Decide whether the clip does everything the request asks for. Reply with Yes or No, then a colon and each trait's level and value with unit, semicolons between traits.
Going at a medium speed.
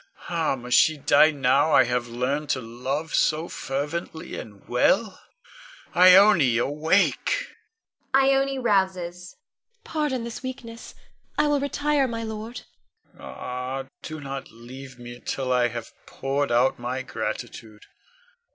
No: slow, 130 wpm